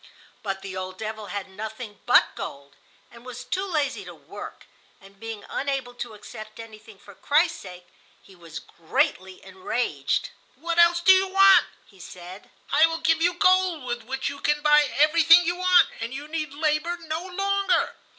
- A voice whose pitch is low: No, very high, 265 Hz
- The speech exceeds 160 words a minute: Yes, average, 175 wpm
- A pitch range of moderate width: No, wide, 8.4 semitones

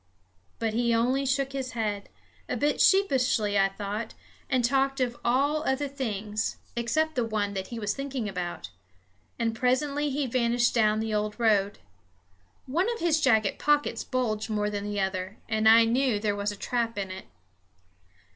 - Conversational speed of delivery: Yes, average, 165 wpm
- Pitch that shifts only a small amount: No, average, 4.2 semitones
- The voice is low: No, high, 230 Hz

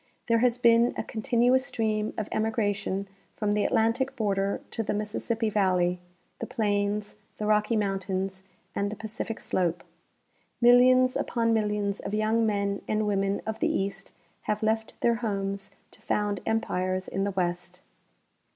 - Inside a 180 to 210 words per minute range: No, average, 150 wpm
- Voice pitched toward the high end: Yes, high, 210 Hz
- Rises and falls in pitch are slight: Yes, narrow, 2.3 semitones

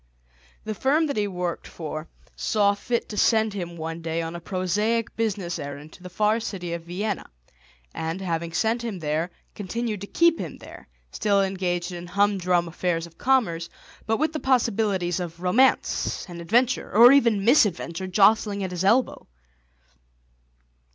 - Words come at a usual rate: Yes, average, 160 wpm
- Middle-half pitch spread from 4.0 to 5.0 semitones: Yes, average, 4.4 semitones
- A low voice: No, high, 190 Hz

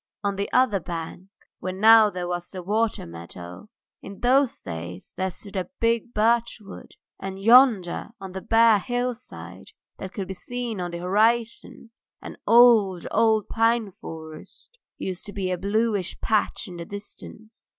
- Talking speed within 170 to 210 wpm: No, average, 155 wpm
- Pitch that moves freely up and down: No, average, 3.9 semitones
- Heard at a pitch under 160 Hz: No, high, 200 Hz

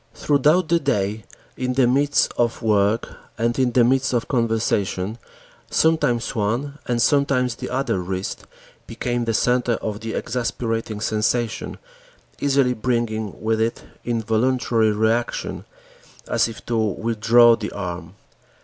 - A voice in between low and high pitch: No, low, 115 Hz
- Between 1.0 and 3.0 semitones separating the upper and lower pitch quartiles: Yes, narrow, 2.5 semitones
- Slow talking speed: Yes, slow, 130 wpm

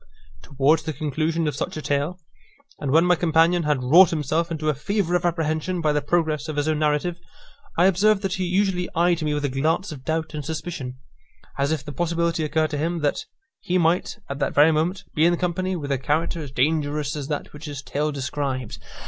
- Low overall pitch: No, medium, 155 Hz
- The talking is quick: Yes, fast, 215 wpm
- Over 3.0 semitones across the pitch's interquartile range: No, average, 2.7 semitones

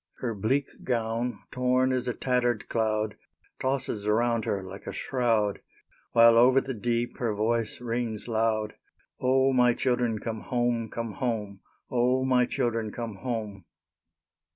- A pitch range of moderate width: No, narrow, 2.3 semitones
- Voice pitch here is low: Yes, low, 115 Hz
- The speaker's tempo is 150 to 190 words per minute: No, average, 140 wpm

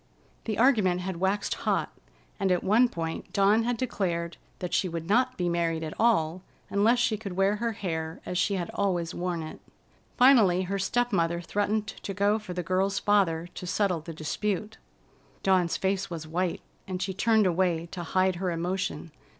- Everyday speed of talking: Yes, average, 180 wpm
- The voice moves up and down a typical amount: Yes, average, 3.2 semitones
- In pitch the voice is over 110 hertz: Yes, high, 190 Hz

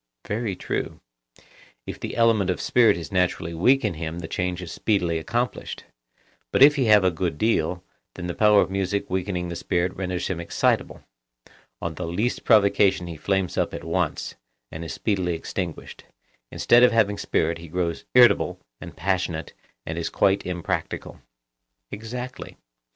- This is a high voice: No, very low, 90 Hz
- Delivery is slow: No, average, 160 wpm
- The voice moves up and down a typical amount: Yes, average, 3.9 semitones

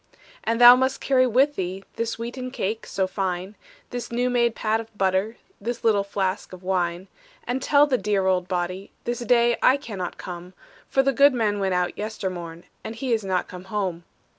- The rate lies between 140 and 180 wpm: No, average, 190 wpm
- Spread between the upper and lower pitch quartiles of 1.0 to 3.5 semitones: No, average, 4.4 semitones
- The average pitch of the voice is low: No, high, 210 Hz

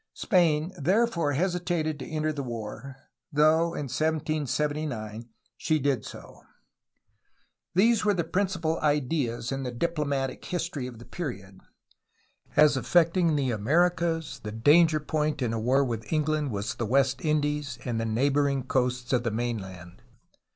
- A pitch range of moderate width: Yes, average, 4.6 semitones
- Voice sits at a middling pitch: Yes, medium, 145 Hz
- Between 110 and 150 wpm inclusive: Yes, average, 140 wpm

